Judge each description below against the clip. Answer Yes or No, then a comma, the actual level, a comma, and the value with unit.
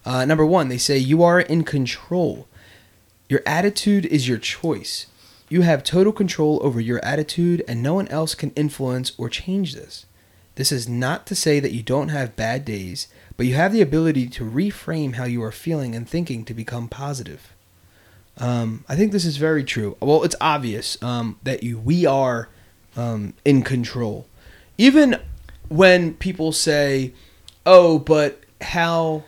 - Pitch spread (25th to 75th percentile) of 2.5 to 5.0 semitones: No, wide, 5.6 semitones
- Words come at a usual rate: Yes, average, 170 wpm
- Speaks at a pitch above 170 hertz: No, low, 135 Hz